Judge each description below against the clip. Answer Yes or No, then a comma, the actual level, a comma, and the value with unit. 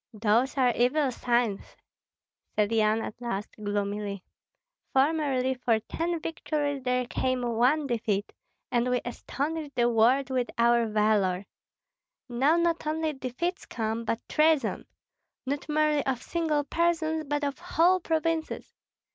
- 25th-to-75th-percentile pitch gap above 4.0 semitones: Yes, average, 5.0 semitones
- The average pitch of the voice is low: No, very high, 255 Hz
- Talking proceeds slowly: Yes, slow, 130 wpm